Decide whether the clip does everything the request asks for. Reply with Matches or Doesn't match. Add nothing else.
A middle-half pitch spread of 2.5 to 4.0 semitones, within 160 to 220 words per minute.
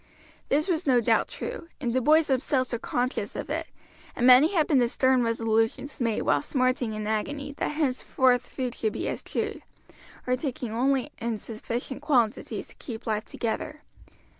Matches